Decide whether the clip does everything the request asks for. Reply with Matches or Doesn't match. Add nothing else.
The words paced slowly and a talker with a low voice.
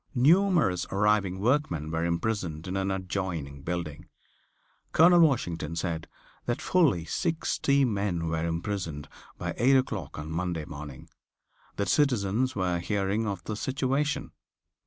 Matches